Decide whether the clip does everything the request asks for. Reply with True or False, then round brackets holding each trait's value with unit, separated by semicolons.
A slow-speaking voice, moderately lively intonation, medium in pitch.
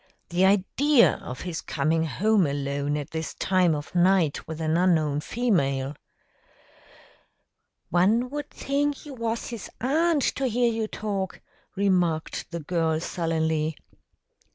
False (130 wpm; 6.3 semitones; 180 Hz)